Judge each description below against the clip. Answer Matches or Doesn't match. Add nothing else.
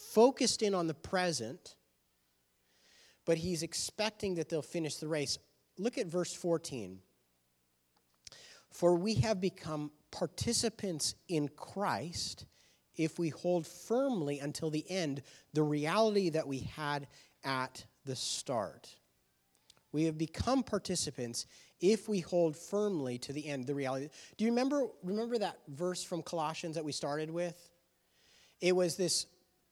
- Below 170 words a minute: Matches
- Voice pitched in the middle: Matches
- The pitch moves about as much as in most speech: Matches